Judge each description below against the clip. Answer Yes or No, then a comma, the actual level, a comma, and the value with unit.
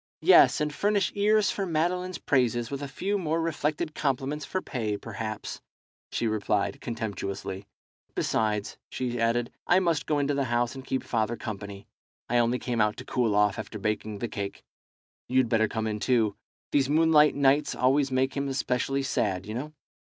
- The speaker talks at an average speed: Yes, average, 175 wpm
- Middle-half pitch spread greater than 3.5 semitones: Yes, average, 5.2 semitones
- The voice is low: Yes, low, 125 Hz